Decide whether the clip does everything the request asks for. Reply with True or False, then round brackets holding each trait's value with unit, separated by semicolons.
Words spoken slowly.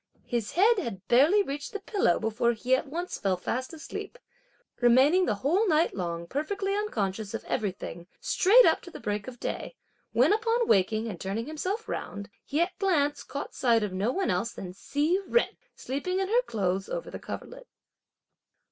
False (185 wpm)